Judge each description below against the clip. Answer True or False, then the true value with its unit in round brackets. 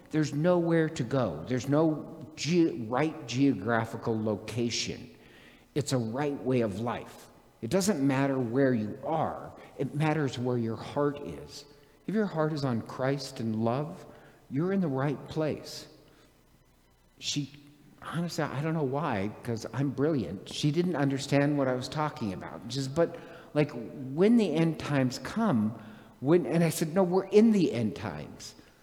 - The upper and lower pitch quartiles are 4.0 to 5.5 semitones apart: True (4.4 semitones)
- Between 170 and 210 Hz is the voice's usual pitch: False (140 Hz)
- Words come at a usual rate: True (160 wpm)